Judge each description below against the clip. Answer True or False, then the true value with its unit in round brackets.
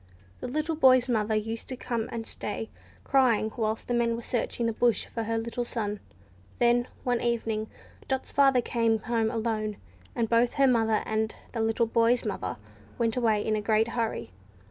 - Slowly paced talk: False (180 wpm)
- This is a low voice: False (230 Hz)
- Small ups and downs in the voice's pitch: True (1.7 semitones)